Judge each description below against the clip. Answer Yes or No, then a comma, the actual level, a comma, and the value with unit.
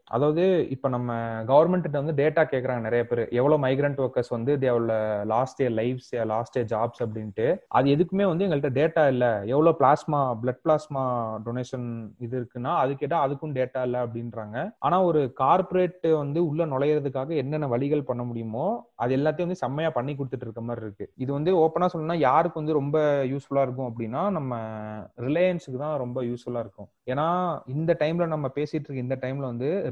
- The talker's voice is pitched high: No, low, 135 Hz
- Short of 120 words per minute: No, average, 125 wpm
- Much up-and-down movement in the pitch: No, average, 4.3 semitones